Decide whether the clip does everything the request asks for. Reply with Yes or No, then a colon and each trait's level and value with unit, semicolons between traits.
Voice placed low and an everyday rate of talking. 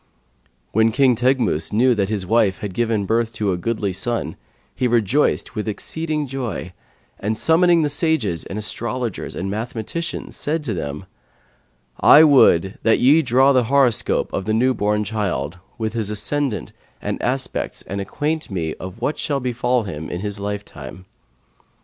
Yes: low, 110 Hz; average, 155 wpm